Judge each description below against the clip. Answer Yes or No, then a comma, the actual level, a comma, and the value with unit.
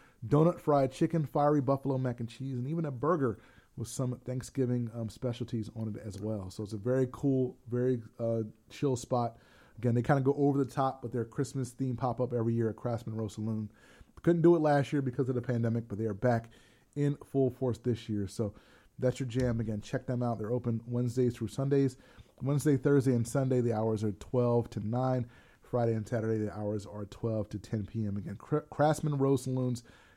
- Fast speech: Yes, fast, 210 wpm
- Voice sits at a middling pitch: No, low, 125 Hz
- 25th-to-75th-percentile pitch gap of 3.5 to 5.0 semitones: No, average, 3.1 semitones